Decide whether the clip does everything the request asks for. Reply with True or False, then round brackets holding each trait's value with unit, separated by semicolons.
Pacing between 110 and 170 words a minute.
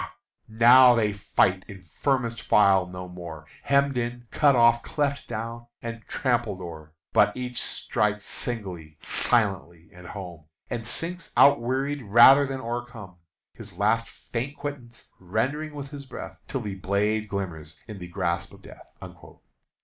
True (140 wpm)